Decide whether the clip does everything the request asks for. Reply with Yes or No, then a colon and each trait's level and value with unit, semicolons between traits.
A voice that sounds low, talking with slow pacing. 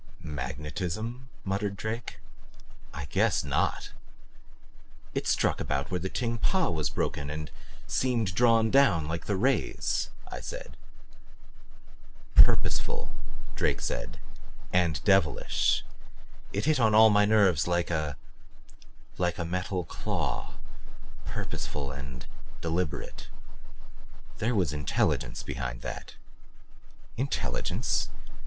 Yes: very low, 90 Hz; slow, 105 wpm